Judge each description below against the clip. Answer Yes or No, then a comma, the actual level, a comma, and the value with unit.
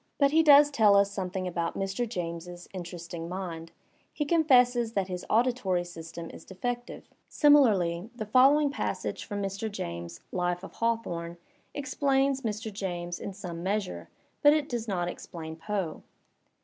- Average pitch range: No, wide, 5.8 semitones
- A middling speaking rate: Yes, average, 150 wpm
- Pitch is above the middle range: Yes, high, 195 Hz